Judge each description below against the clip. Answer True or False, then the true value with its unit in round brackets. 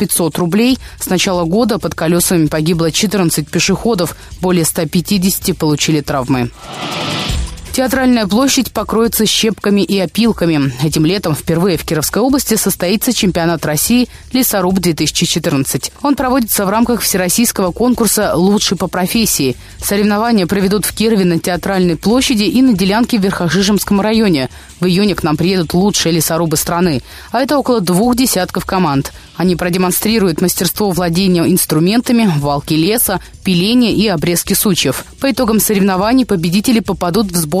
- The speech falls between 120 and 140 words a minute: True (135 wpm)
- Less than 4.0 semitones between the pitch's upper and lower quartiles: False (4.3 semitones)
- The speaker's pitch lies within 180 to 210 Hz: True (185 Hz)